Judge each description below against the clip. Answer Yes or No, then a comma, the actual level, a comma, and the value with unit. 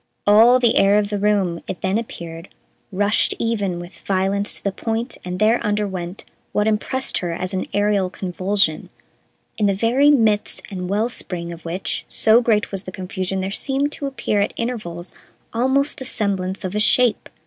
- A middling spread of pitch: Yes, average, 3.4 semitones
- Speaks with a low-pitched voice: No, high, 205 Hz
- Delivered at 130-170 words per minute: No, average, 180 wpm